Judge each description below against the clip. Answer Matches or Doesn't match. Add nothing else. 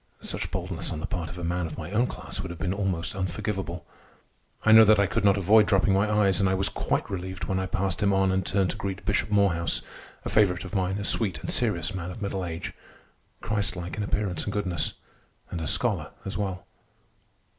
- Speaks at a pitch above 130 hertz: Doesn't match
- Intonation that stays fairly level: Matches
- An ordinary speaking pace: Doesn't match